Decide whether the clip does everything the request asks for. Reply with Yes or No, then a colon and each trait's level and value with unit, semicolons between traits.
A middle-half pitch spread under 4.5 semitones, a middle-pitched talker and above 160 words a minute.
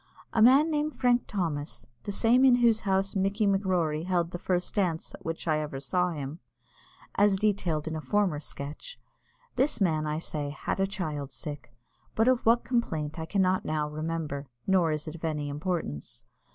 No: average, 5.1 semitones; medium, 175 Hz; average, 180 wpm